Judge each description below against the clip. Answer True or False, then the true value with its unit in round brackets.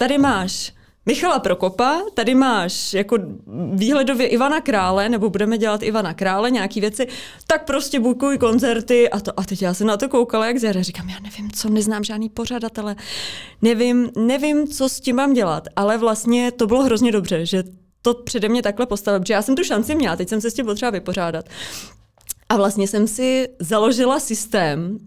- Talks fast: True (185 wpm)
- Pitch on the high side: True (220 Hz)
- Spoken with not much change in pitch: False (3.9 semitones)